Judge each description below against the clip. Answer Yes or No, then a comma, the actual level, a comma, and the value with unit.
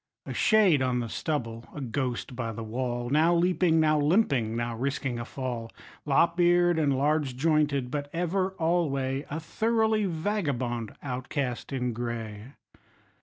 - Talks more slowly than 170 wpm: Yes, average, 145 wpm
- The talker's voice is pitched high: No, medium, 140 Hz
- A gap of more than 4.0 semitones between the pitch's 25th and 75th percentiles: Yes, average, 5.2 semitones